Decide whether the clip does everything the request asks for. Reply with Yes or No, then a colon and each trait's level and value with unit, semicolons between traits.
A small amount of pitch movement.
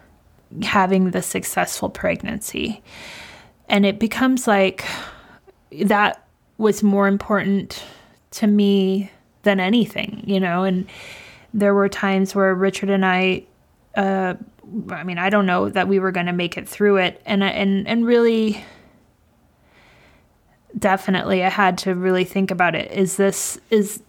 Yes: narrow, 1.8 semitones